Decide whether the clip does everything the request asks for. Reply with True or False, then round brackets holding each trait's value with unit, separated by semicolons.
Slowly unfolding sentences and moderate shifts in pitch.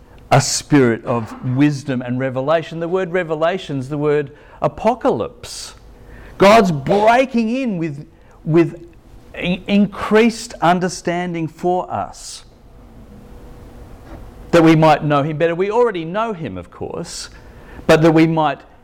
True (120 wpm; 4.5 semitones)